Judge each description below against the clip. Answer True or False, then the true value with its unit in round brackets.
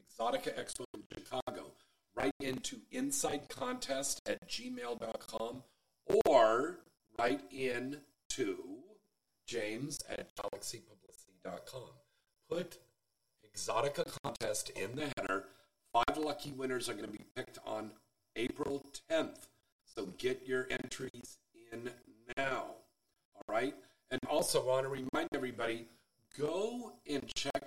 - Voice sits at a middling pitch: True (145 Hz)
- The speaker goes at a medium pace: False (115 wpm)